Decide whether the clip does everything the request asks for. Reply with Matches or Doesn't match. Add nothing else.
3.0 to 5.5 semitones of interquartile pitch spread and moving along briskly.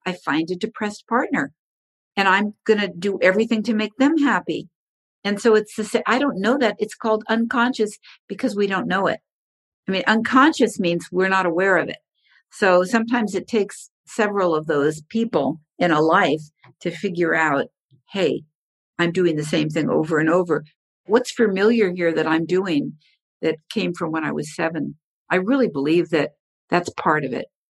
Doesn't match